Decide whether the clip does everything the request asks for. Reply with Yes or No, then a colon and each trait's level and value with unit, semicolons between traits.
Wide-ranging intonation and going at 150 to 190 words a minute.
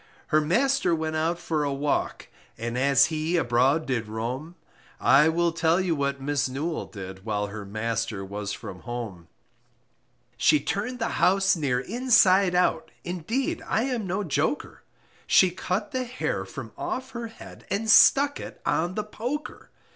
Yes: wide, 8.0 semitones; average, 160 wpm